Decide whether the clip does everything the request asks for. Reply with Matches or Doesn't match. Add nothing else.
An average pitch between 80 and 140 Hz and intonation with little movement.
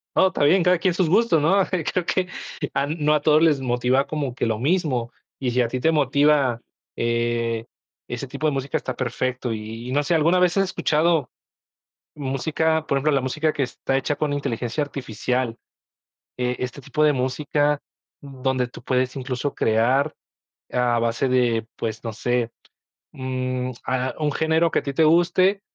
Doesn't match